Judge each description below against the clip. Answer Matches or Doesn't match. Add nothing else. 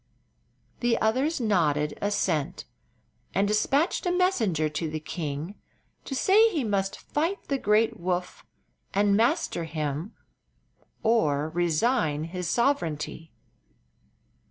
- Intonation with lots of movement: Matches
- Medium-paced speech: Doesn't match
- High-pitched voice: Matches